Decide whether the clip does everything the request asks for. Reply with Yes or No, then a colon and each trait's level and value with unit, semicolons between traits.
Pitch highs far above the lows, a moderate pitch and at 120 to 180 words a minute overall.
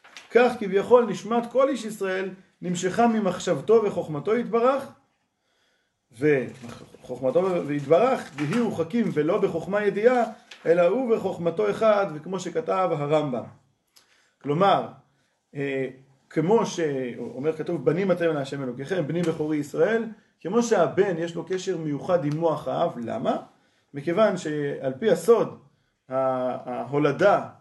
No: wide, 6.6 semitones; medium, 175 Hz; average, 110 wpm